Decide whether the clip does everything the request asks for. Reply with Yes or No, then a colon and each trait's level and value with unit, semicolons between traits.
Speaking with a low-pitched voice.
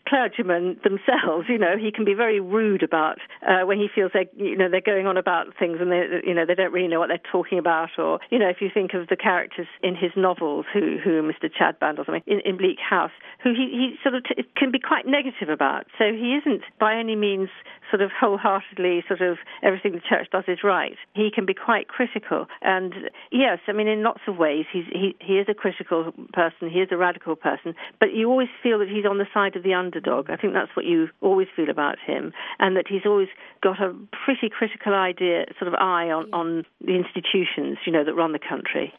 No: high, 195 Hz